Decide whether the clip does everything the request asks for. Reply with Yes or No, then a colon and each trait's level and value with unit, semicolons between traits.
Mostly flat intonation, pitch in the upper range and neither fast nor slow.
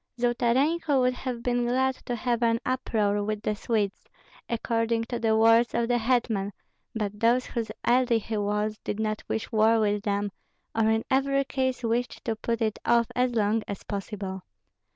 Yes: narrow, 2.3 semitones; high, 230 Hz; average, 180 wpm